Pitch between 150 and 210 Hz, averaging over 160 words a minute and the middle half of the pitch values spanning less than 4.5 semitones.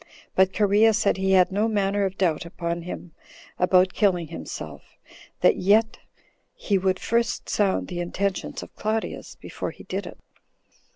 No: high, 190 Hz; average, 155 wpm; narrow, 2.4 semitones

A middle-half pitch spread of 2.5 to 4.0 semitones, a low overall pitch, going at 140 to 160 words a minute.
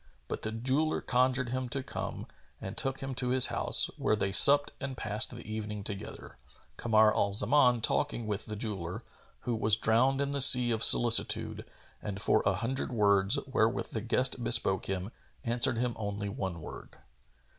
No: average, 3.6 semitones; low, 115 Hz; average, 175 wpm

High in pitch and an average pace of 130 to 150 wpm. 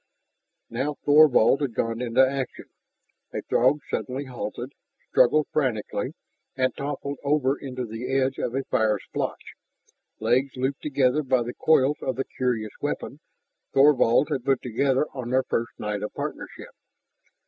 No: low, 130 Hz; average, 145 wpm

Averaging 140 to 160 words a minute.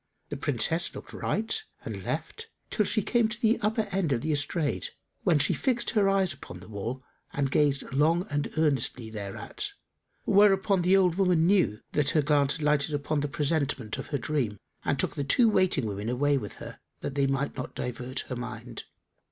No: average, 195 wpm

